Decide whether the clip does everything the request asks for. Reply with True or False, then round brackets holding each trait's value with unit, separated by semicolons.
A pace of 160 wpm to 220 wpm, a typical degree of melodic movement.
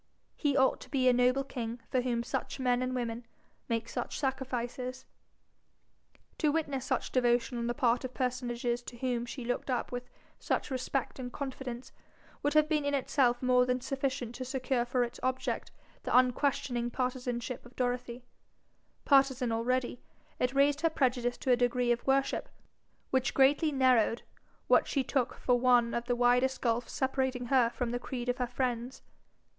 False (170 wpm; 1.5 semitones)